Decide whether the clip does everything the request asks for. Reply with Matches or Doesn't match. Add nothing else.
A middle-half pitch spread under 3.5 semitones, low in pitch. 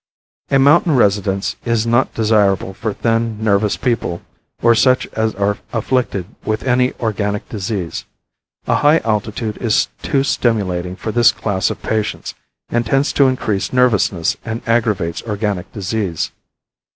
Matches